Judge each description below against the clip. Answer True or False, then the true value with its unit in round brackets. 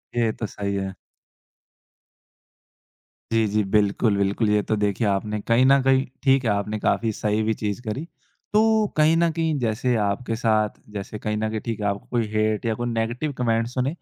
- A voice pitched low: True (110 Hz)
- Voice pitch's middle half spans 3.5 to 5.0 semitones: False (2.9 semitones)